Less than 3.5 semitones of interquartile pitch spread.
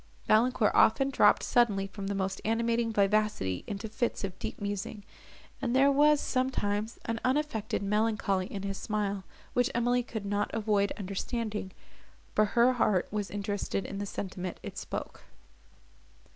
Yes: average, 2.9 semitones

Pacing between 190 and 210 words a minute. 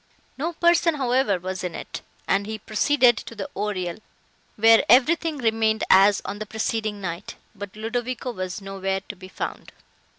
No: average, 160 wpm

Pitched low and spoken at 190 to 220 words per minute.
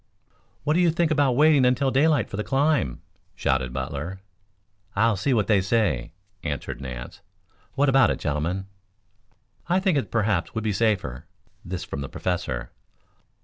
No: low, 105 Hz; average, 155 wpm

